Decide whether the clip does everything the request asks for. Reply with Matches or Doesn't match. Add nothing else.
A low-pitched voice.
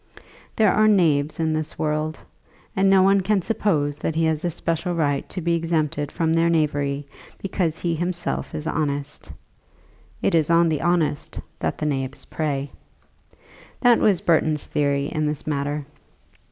Doesn't match